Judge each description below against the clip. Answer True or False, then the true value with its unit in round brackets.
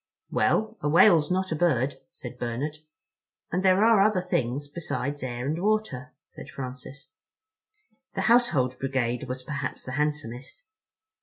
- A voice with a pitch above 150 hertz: False (145 Hz)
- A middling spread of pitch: False (6.0 semitones)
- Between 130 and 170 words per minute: True (140 wpm)